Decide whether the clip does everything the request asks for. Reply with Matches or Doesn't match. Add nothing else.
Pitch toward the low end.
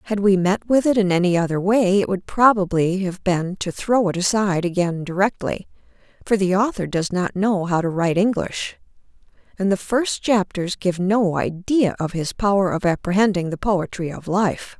Doesn't match